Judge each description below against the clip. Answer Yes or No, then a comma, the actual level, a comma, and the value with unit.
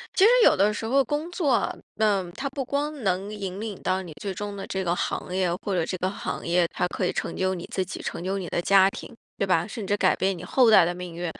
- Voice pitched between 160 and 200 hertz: Yes, high, 195 Hz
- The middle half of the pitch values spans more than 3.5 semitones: No, average, 3.2 semitones